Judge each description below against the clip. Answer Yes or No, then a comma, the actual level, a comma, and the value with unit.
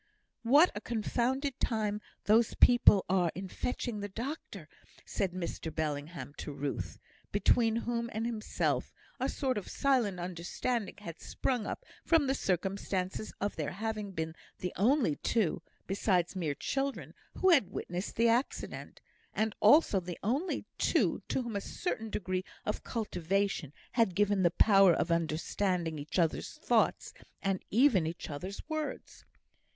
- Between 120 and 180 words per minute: Yes, average, 145 wpm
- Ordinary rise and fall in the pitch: Yes, average, 5.0 semitones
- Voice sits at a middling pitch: No, high, 205 Hz